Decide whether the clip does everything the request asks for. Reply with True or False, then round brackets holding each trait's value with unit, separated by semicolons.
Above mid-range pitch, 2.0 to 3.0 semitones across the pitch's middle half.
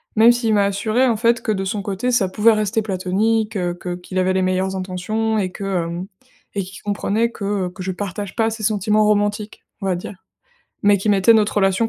True (205 Hz; 2.7 semitones)